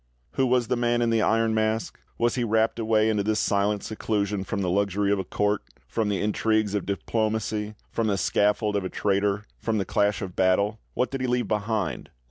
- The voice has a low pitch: Yes, low, 105 Hz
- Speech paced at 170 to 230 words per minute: Yes, fast, 205 wpm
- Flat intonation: Yes, narrow, 1.8 semitones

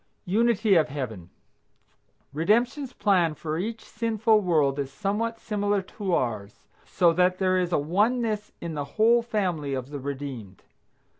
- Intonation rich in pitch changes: Yes, wide, 6.9 semitones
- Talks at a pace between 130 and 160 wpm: Yes, average, 145 wpm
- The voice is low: No, medium, 185 Hz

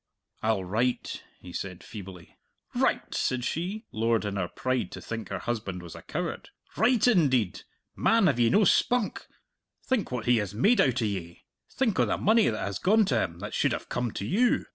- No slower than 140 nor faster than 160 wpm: No, average, 200 wpm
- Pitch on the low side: Yes, low, 120 Hz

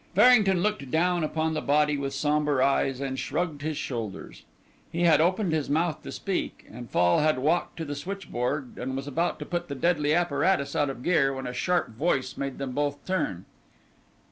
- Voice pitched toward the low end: No, medium, 150 Hz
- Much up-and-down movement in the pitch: No, average, 4.1 semitones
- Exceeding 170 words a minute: Yes, average, 195 wpm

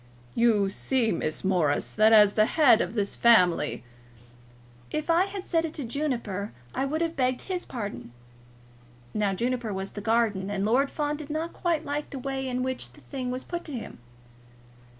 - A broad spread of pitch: Yes, wide, 6.3 semitones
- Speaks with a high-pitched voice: Yes, high, 240 Hz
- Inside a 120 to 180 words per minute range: No, average, 190 wpm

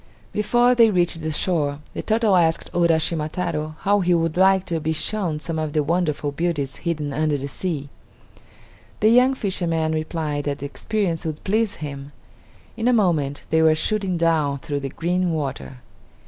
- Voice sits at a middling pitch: Yes, medium, 165 Hz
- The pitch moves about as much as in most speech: Yes, average, 3.6 semitones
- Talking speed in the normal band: Yes, average, 175 wpm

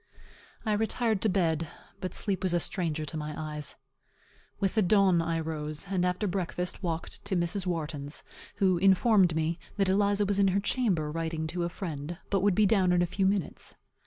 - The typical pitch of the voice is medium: Yes, medium, 180 Hz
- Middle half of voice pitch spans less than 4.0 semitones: Yes, average, 3.5 semitones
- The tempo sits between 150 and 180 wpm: No, average, 190 wpm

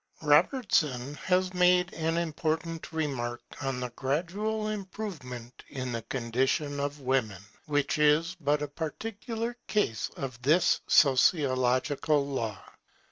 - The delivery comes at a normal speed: No, slow, 115 wpm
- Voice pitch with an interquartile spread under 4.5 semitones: No, average, 5.3 semitones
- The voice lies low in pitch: No, medium, 150 Hz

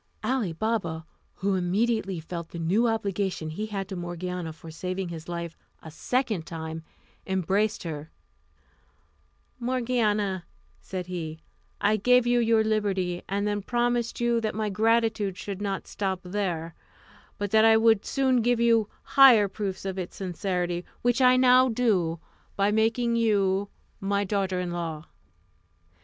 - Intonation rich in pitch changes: No, average, 4.1 semitones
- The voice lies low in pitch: No, high, 200 Hz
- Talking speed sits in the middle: Yes, average, 145 wpm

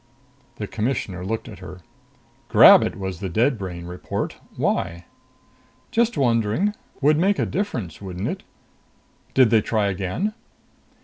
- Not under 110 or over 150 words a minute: Yes, slow, 135 wpm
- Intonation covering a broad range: Yes, wide, 6.5 semitones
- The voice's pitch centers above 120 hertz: No, low, 105 Hz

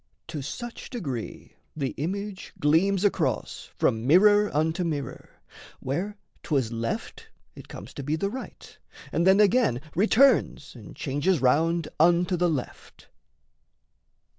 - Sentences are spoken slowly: Yes, slow, 125 wpm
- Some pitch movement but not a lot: No, wide, 6.0 semitones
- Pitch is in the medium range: Yes, medium, 165 Hz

